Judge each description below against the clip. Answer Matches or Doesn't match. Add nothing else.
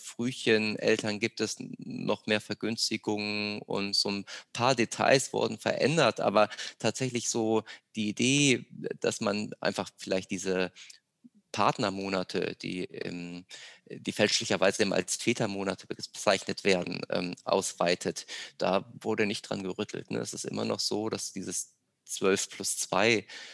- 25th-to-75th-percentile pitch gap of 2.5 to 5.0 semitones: Matches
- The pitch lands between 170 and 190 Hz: Doesn't match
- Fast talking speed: Doesn't match